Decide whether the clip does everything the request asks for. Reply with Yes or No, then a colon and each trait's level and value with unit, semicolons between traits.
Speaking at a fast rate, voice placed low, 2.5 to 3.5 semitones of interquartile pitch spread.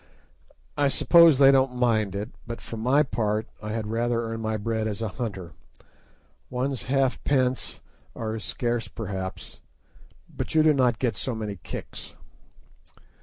No: average, 155 wpm; low, 115 Hz; average, 3.1 semitones